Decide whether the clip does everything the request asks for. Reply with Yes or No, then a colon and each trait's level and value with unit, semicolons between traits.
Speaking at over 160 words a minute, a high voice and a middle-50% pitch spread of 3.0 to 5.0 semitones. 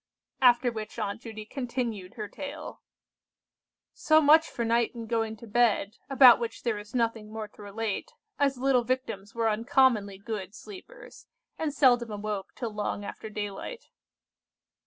No: average, 155 wpm; high, 230 Hz; average, 3.3 semitones